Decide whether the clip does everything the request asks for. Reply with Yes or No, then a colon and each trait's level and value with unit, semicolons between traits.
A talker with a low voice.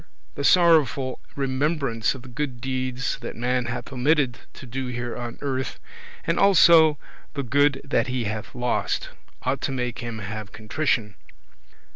Yes: low, 130 Hz